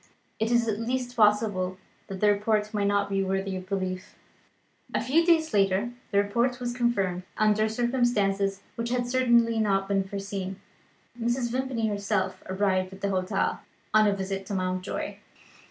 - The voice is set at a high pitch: Yes, high, 205 Hz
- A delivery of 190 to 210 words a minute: No, average, 160 wpm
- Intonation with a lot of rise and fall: No, average, 3.5 semitones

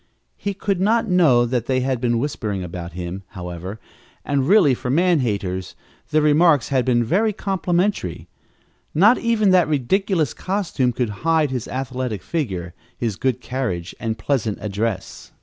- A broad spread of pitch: Yes, wide, 8.1 semitones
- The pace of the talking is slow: No, average, 150 wpm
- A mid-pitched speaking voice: No, low, 130 Hz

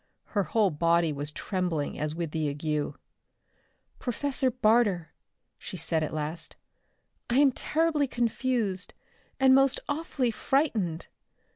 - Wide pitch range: Yes, wide, 8.4 semitones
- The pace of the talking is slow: Yes, slow, 120 wpm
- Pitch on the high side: Yes, high, 200 Hz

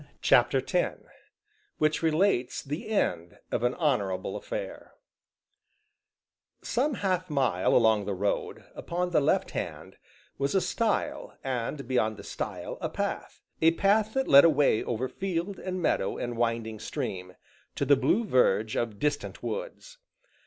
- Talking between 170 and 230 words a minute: No, average, 140 wpm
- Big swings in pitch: Yes, wide, 8.4 semitones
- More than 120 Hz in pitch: Yes, medium, 140 Hz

